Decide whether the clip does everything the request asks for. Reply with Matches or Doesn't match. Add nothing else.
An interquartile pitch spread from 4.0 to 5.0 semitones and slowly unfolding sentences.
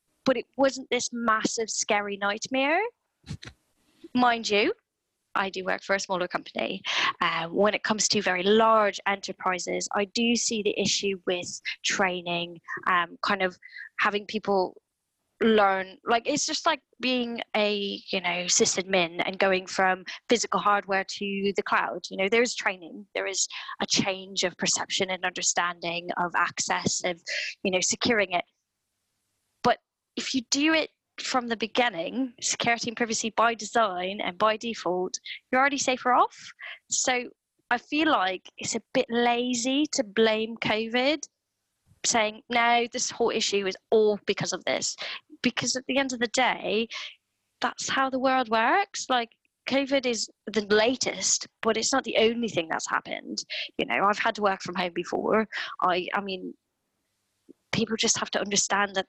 Doesn't match